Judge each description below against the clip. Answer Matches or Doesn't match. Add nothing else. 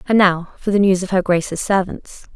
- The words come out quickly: Matches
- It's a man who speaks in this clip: Doesn't match